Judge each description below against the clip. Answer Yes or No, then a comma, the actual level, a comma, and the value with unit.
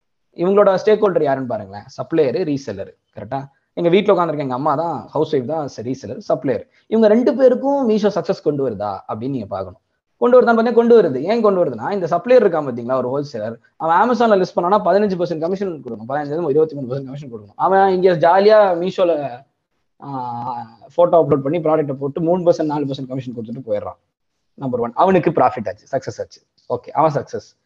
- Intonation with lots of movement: Yes, wide, 6.6 semitones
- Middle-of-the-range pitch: Yes, medium, 165 Hz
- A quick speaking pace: Yes, fast, 155 wpm